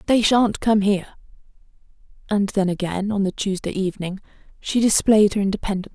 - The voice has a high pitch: Yes, high, 200 Hz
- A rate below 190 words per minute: Yes, average, 150 wpm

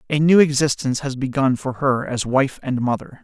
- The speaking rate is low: No, fast, 205 wpm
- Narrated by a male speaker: Yes, male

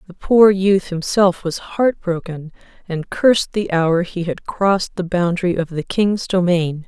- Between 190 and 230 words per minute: No, average, 175 wpm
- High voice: No, medium, 180 Hz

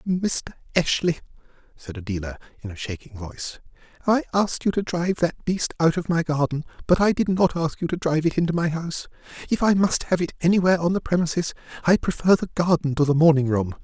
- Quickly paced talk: Yes, fast, 210 wpm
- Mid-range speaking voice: Yes, medium, 160 Hz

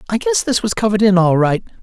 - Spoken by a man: Yes, male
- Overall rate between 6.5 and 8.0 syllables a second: Yes, 6.8 syllables/s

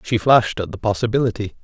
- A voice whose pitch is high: No, low, 110 Hz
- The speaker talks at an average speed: Yes, average, 185 wpm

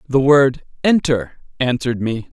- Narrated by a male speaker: Yes, male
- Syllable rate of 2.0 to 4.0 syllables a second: No, 4.4 syllables/s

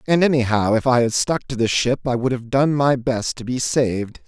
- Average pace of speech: No, fast, 255 wpm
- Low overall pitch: Yes, low, 125 Hz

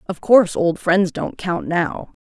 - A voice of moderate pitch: Yes, medium, 180 Hz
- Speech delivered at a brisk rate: No, average, 185 wpm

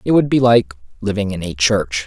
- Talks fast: Yes, fast, 235 wpm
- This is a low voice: Yes, low, 105 Hz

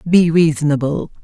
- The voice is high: No, medium, 160 Hz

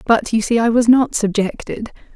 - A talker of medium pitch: No, high, 225 Hz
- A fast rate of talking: No, average, 195 wpm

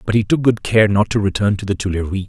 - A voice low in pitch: Yes, low, 105 Hz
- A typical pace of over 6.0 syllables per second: Yes, 6.5 syllables/s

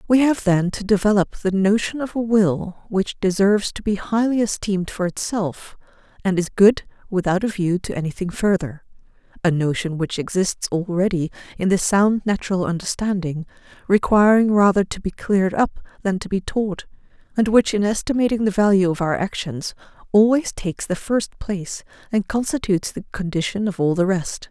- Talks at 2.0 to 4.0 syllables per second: No, 5.2 syllables/s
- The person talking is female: Yes, female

